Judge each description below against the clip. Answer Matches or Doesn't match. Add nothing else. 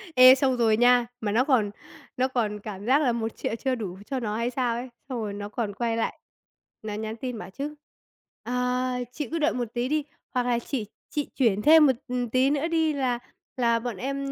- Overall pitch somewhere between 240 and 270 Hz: Matches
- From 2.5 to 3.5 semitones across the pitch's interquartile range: Matches